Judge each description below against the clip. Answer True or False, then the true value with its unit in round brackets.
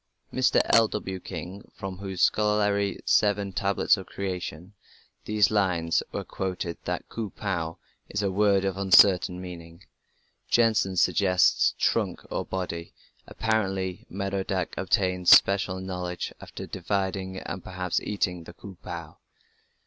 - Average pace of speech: False (125 wpm)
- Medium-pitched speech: False (95 Hz)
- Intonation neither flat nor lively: False (1.9 semitones)